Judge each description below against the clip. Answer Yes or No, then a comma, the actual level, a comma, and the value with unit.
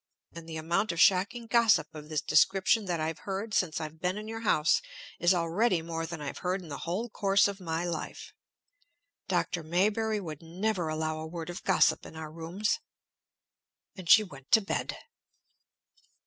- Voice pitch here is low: No, medium, 175 Hz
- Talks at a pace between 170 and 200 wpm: Yes, average, 175 wpm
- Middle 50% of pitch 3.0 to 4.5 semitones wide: Yes, average, 3.9 semitones